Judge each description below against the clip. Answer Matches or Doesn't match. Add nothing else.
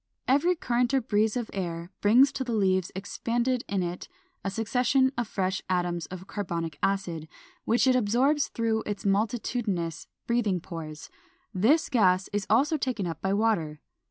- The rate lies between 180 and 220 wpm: Doesn't match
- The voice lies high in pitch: Matches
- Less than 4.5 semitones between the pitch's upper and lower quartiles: Doesn't match